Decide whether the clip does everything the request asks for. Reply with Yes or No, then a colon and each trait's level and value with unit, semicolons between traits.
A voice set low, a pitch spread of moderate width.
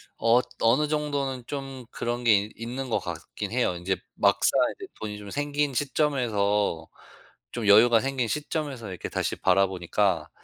Yes: low, 120 Hz; average, 4.9 semitones